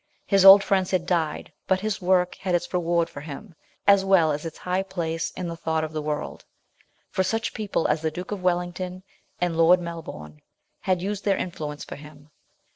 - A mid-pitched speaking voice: Yes, medium, 175 Hz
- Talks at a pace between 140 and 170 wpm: No, average, 195 wpm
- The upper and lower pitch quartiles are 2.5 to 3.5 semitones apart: Yes, average, 2.8 semitones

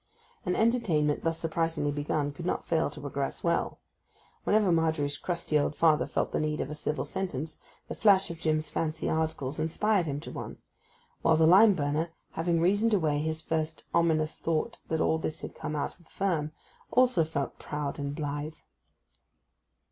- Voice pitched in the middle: Yes, medium, 160 Hz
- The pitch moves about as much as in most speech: No, narrow, 2.1 semitones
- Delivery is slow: No, average, 175 wpm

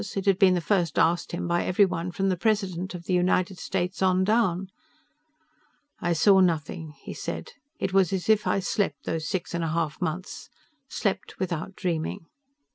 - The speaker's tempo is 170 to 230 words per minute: Yes, average, 180 wpm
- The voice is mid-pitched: Yes, medium, 180 Hz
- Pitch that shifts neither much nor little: No, narrow, 2.1 semitones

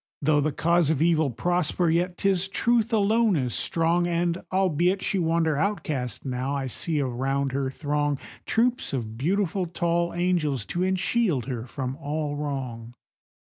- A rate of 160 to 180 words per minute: No, average, 150 wpm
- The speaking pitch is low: No, medium, 160 Hz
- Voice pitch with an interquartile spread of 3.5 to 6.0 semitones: Yes, average, 4.6 semitones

